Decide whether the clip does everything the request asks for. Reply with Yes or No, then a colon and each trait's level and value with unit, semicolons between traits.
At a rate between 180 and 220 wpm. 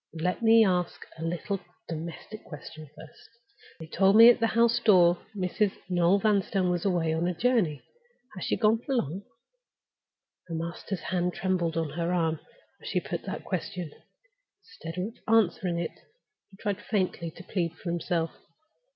No: average, 165 wpm